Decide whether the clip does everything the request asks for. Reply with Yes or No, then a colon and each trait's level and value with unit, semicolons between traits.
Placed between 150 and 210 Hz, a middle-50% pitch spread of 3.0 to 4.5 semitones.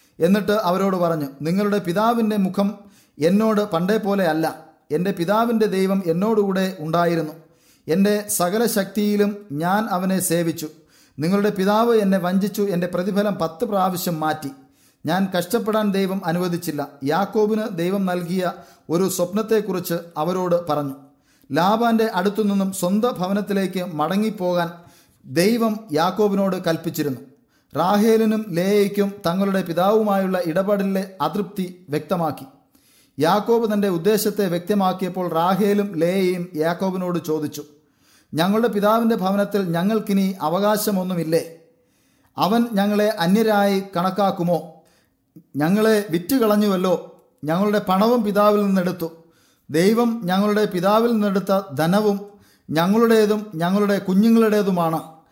Yes: high, 190 Hz; average, 3.8 semitones